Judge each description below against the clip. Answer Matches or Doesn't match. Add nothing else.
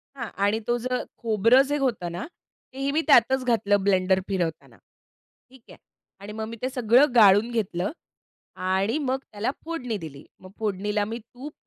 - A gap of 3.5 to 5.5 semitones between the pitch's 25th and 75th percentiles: Matches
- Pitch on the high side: Matches